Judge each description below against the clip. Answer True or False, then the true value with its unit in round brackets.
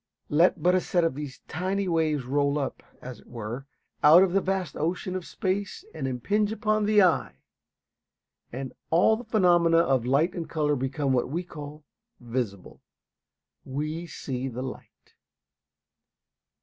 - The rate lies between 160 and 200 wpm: False (150 wpm)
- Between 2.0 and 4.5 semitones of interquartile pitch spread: False (5.5 semitones)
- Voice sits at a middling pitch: True (155 Hz)